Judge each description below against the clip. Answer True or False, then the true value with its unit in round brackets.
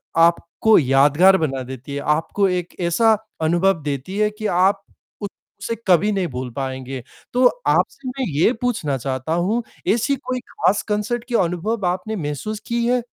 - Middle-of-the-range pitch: True (180 Hz)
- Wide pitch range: True (6.9 semitones)